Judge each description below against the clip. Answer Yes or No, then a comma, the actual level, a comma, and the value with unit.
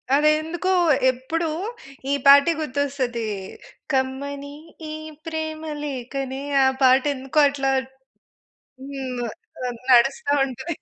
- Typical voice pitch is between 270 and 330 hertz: Yes, very high, 275 Hz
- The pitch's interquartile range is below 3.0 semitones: Yes, narrow, 2.6 semitones